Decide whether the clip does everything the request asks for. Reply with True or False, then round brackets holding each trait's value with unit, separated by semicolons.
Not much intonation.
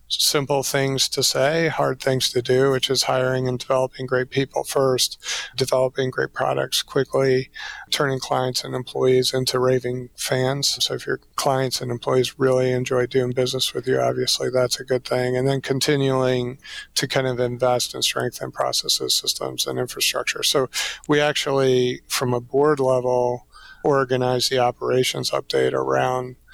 True (1.2 semitones)